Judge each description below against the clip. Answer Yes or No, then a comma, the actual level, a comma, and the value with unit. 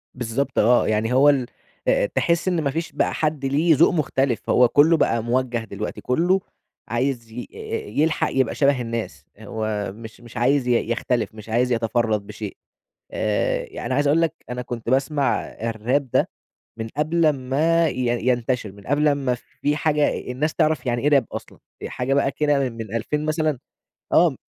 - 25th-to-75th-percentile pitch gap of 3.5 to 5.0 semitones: Yes, average, 4.1 semitones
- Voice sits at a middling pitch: No, low, 130 Hz